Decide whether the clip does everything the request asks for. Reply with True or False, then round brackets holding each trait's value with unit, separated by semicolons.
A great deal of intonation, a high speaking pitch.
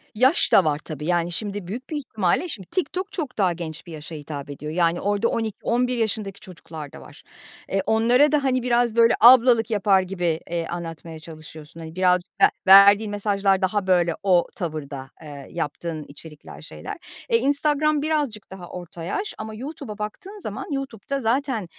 True (6.5 semitones; 200 Hz)